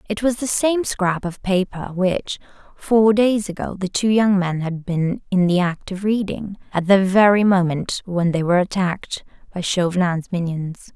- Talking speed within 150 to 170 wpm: No, average, 180 wpm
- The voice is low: No, high, 190 Hz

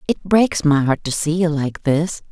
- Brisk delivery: Yes, fast, 235 wpm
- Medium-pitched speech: Yes, medium, 160 Hz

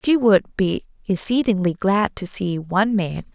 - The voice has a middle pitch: No, high, 200 Hz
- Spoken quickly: No, average, 160 wpm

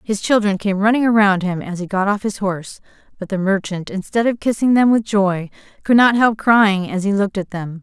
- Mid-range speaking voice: No, high, 200 Hz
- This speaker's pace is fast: Yes, fast, 230 wpm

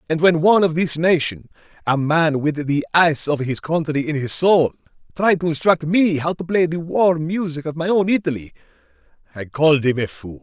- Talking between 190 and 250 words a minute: Yes, average, 195 wpm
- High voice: No, medium, 155 Hz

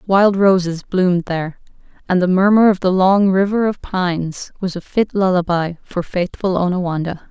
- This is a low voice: No, medium, 185 Hz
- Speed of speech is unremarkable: Yes, average, 165 wpm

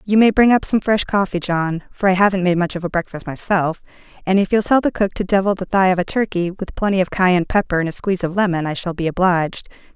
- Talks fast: Yes, fast, 265 wpm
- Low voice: No, medium, 185 Hz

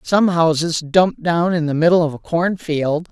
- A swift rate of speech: No, average, 195 wpm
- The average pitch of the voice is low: No, medium, 165 Hz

